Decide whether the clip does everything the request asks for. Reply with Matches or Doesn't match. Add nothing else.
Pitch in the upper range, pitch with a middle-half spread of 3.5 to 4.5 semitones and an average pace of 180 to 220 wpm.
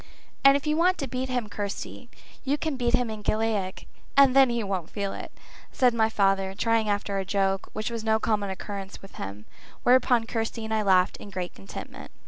Matches